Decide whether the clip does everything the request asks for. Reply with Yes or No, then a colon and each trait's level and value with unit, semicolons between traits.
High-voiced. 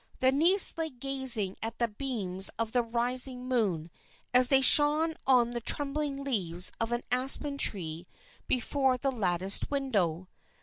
Yes: very high, 250 Hz